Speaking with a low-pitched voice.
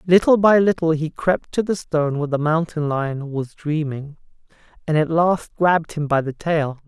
No: medium, 160 Hz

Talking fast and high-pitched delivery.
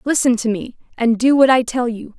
Yes: fast, 245 wpm; high, 240 Hz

